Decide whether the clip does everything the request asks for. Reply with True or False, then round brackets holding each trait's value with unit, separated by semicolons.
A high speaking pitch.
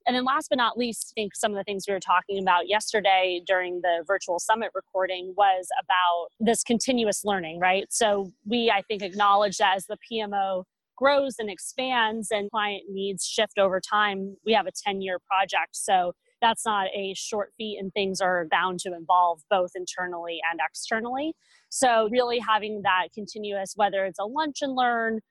True (200 Hz)